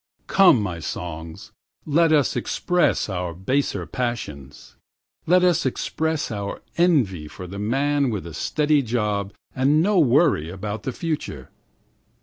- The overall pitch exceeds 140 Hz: No, low, 120 Hz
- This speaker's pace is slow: Yes, slow, 130 wpm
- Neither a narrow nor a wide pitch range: No, wide, 8.4 semitones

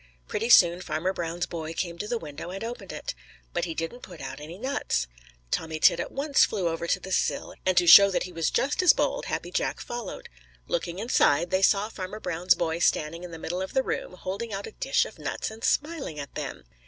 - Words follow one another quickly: Yes, fast, 230 wpm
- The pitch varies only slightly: No, average, 4.9 semitones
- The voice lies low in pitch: No, medium, 180 Hz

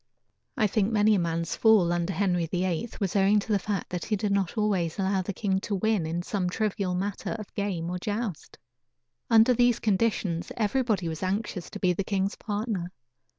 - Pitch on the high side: Yes, high, 195 Hz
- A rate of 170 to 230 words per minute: Yes, average, 195 wpm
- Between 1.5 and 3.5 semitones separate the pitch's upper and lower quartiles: Yes, average, 3.0 semitones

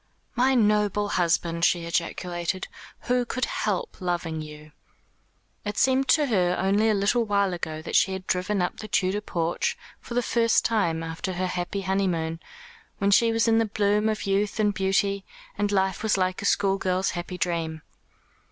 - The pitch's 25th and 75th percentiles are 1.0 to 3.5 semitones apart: Yes, average, 3.1 semitones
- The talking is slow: No, average, 175 wpm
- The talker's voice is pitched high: Yes, high, 195 Hz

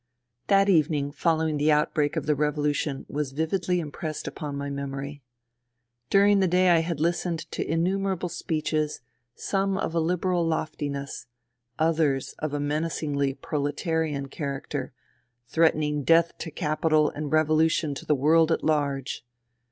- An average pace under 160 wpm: Yes, average, 145 wpm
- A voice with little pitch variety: Yes, narrow, 2.3 semitones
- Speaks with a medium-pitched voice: Yes, medium, 155 Hz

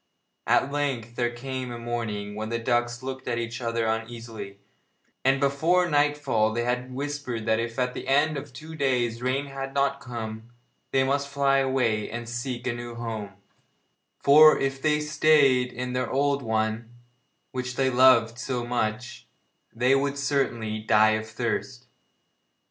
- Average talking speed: Yes, average, 160 wpm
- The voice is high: No, low, 125 Hz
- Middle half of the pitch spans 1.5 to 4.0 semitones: Yes, average, 3.1 semitones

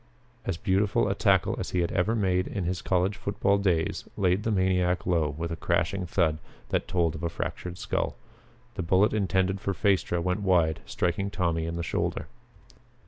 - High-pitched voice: No, very low, 90 Hz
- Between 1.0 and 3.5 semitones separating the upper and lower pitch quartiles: Yes, narrow, 2.5 semitones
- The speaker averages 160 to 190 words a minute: Yes, average, 185 wpm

